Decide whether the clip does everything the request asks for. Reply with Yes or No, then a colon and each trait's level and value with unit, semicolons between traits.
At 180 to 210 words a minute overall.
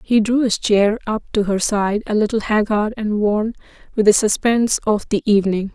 Yes: average, 200 wpm